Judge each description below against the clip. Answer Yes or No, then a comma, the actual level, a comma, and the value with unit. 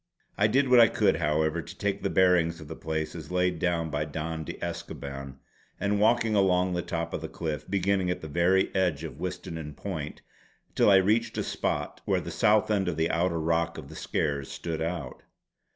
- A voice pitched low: Yes, very low, 85 Hz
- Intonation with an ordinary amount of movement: Yes, average, 3.4 semitones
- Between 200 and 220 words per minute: Yes, fast, 205 wpm